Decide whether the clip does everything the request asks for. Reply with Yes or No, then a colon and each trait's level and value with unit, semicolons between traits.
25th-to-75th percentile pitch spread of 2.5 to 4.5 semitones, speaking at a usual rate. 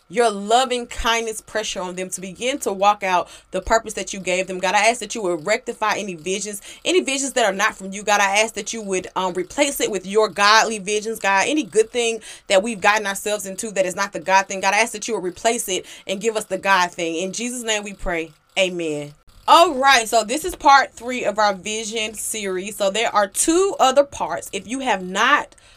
No: average, 3.2 semitones; fast, 240 wpm